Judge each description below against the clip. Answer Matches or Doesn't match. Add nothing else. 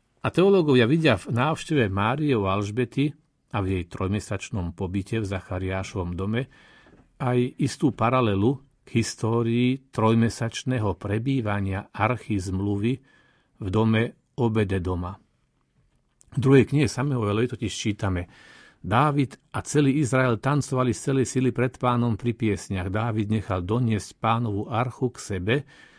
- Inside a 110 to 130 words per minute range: Matches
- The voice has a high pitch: Doesn't match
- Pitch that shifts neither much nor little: Matches